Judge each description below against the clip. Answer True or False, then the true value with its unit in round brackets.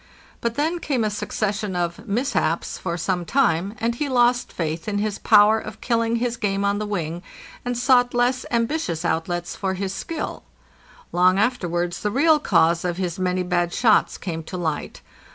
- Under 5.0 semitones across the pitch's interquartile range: False (5.5 semitones)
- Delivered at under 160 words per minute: False (180 wpm)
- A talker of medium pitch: False (205 Hz)